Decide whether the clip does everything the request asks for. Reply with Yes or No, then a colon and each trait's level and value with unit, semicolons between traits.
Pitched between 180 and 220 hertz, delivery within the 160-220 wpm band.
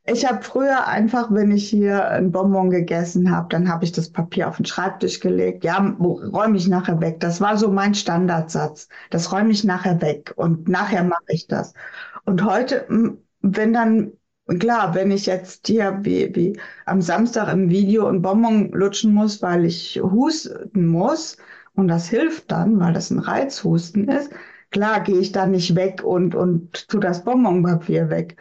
Yes: high, 190 Hz; average, 175 wpm